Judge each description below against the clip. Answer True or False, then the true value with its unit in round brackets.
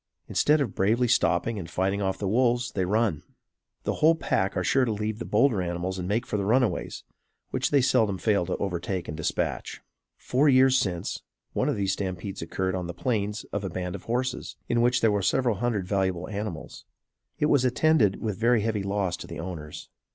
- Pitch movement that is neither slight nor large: True (4.5 semitones)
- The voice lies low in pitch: True (105 Hz)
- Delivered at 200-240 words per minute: True (205 wpm)